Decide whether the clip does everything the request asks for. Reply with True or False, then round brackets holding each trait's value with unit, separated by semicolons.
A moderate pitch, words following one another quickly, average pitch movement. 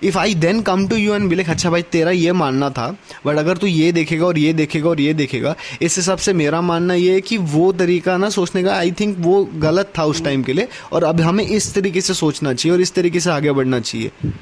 True (175 Hz; 260 wpm; 3.4 semitones)